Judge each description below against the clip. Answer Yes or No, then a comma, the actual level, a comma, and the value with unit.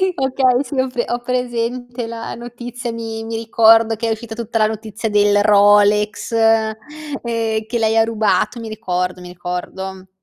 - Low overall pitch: No, high, 225 Hz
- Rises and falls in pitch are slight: Yes, narrow, 2.1 semitones